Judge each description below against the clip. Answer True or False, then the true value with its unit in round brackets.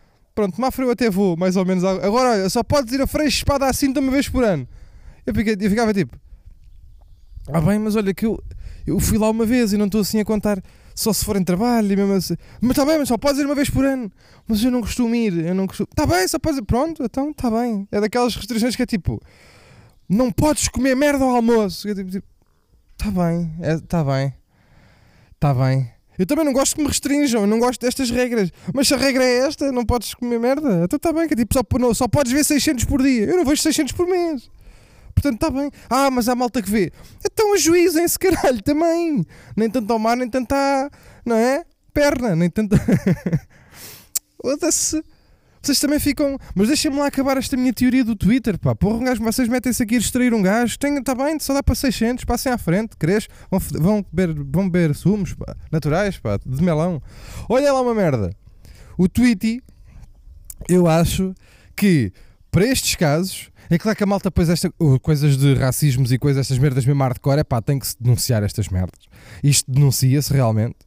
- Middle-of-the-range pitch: False (220 Hz)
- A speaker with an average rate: False (215 wpm)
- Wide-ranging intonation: True (8.5 semitones)